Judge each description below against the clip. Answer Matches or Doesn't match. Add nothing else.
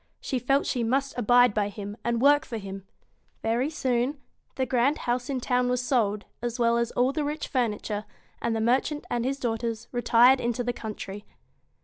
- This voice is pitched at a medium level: Doesn't match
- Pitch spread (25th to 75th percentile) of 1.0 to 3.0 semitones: Matches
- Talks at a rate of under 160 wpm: Doesn't match